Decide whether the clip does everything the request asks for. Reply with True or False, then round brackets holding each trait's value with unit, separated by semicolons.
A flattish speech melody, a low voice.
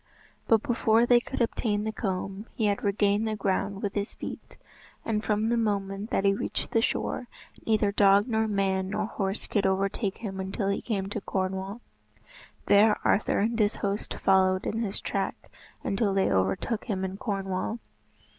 False (2.1 semitones; 205 Hz)